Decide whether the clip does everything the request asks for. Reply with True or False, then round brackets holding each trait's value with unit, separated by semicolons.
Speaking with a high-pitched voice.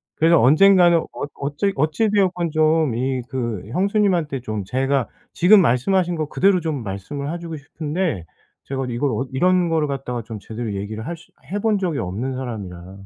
False (145 Hz)